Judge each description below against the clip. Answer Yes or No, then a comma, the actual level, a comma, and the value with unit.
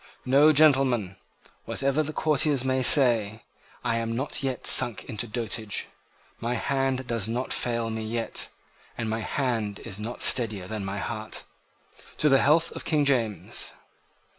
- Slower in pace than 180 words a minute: Yes, average, 150 wpm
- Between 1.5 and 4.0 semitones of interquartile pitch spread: Yes, average, 3.6 semitones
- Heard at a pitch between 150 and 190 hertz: No, low, 120 Hz